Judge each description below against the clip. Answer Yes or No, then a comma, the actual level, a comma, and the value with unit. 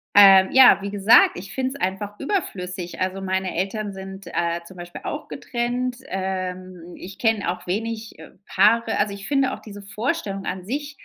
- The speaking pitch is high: Yes, high, 200 Hz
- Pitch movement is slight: No, average, 3.5 semitones